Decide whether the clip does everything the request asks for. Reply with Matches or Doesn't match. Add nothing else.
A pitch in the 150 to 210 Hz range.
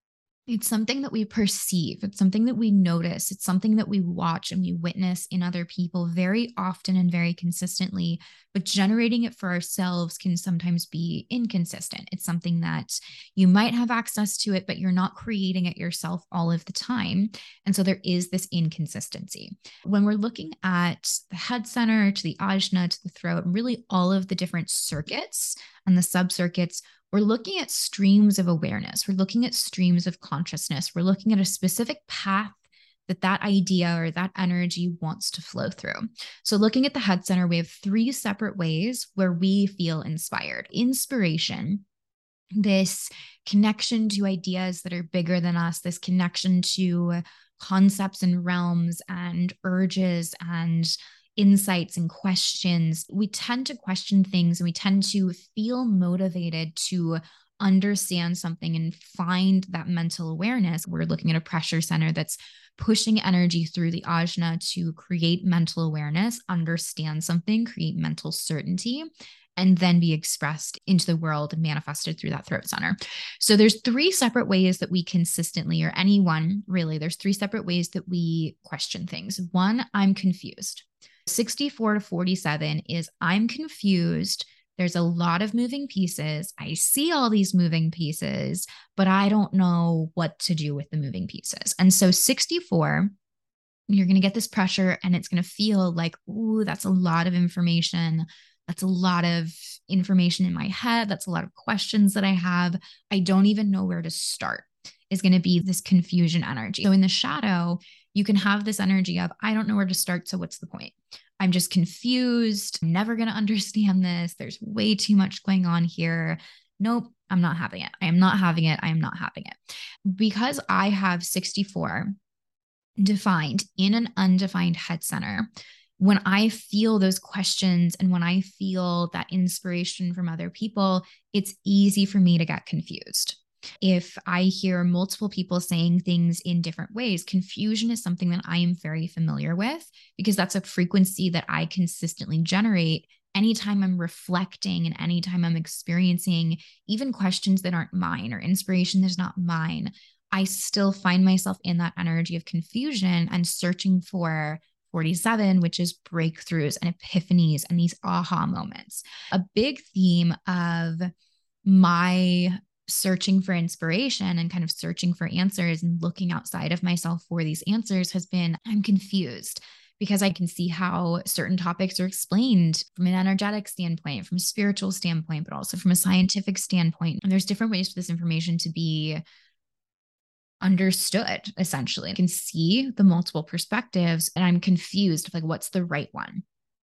Matches